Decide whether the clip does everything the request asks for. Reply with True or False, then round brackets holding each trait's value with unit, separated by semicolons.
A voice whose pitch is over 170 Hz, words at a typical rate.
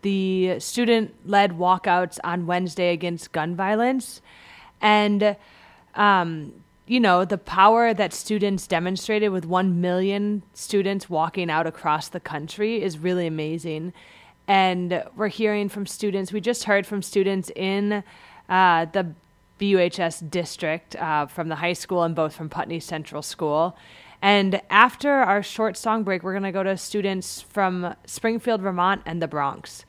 True (185 Hz; 145 wpm)